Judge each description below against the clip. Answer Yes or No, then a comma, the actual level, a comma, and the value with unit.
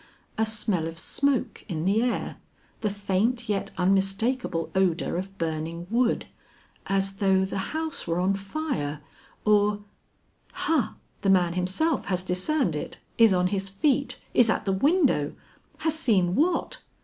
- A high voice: Yes, high, 195 Hz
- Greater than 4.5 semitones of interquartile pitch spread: Yes, average, 4.9 semitones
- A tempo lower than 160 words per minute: Yes, average, 145 wpm